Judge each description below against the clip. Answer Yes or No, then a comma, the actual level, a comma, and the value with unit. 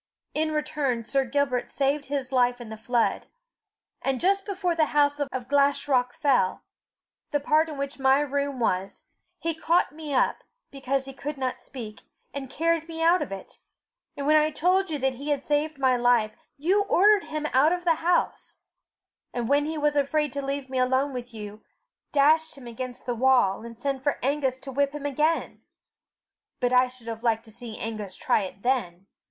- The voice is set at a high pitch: Yes, very high, 275 Hz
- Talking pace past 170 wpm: Yes, average, 190 wpm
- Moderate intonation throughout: Yes, average, 3.4 semitones